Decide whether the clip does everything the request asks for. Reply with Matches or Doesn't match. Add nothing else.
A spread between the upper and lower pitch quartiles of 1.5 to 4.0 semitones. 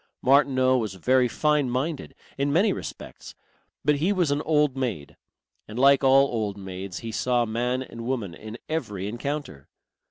Doesn't match